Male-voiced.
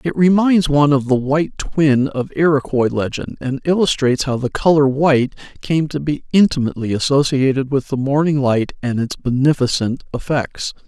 Yes: male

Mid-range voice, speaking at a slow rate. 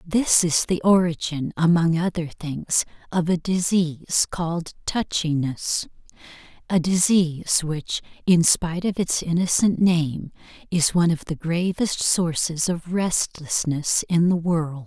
Yes: medium, 170 Hz; slow, 125 wpm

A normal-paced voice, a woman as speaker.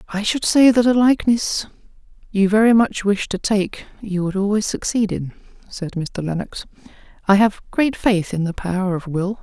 Yes: average, 185 wpm; female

